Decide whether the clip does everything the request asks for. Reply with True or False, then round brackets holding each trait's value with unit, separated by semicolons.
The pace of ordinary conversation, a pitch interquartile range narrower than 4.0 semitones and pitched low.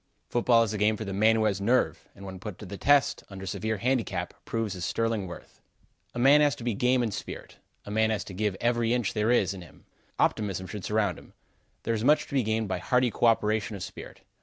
False (240 wpm; 3.1 semitones; 110 Hz)